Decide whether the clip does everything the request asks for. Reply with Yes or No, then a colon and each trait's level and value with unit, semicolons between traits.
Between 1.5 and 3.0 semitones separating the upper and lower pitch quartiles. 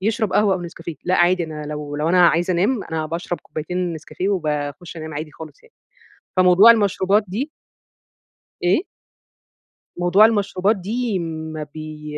No: average, 4.0 semitones